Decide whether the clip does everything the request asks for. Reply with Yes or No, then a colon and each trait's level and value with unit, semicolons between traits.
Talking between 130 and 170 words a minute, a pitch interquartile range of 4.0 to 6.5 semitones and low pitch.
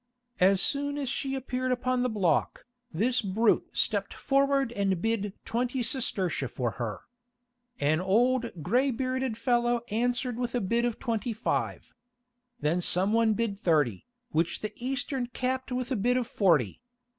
No: average, 155 wpm; average, 4.8 semitones; high, 235 Hz